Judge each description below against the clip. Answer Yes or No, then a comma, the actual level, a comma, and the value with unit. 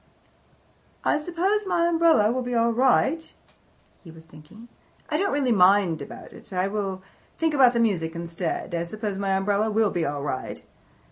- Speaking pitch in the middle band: No, high, 210 Hz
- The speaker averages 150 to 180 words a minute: Yes, average, 165 wpm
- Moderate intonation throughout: No, wide, 7.1 semitones